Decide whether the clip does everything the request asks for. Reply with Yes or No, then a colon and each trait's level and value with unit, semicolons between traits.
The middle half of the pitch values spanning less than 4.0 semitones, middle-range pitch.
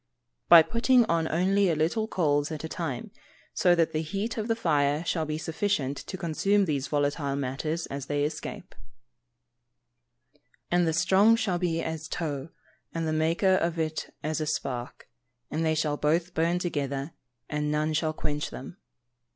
Yes: average, 3.2 semitones; medium, 160 Hz